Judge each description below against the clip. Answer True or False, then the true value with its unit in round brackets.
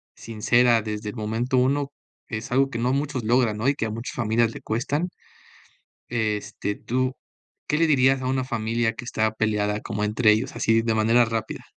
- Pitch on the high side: False (115 Hz)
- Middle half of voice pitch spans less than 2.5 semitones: False (2.8 semitones)